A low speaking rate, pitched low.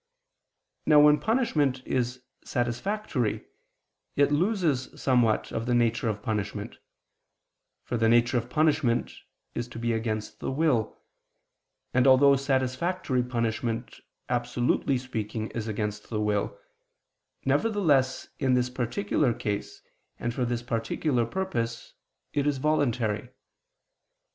Yes: slow, 115 wpm; low, 125 Hz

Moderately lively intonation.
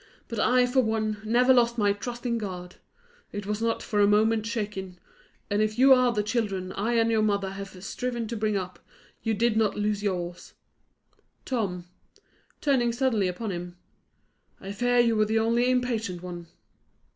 Yes: average, 3.0 semitones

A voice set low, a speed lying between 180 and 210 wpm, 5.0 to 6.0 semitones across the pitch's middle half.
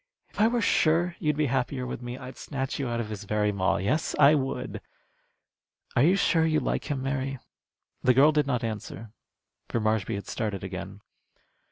Yes: low, 130 Hz; average, 190 wpm; wide, 5.5 semitones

